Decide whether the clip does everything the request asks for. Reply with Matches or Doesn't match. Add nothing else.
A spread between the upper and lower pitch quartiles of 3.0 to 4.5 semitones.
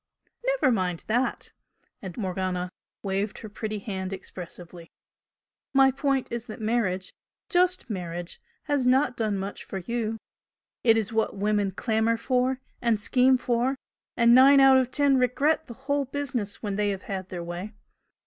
Doesn't match